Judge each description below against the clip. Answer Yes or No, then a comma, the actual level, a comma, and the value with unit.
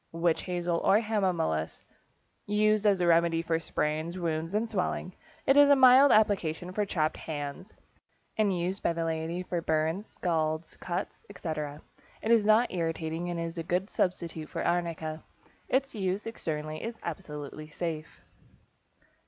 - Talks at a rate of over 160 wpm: No, average, 150 wpm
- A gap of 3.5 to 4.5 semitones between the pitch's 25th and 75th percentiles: Yes, average, 4.1 semitones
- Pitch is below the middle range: No, medium, 170 Hz